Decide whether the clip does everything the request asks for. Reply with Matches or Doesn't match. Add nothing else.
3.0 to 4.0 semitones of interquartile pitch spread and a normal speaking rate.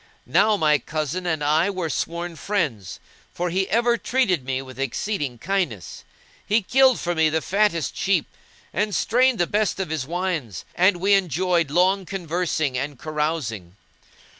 Doesn't match